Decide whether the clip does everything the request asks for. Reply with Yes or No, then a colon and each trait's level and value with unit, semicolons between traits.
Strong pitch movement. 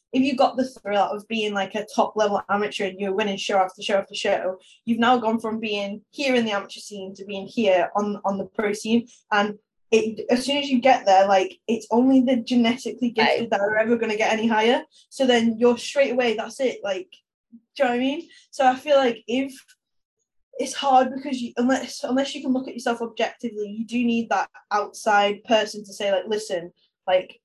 No: average, 3.8 semitones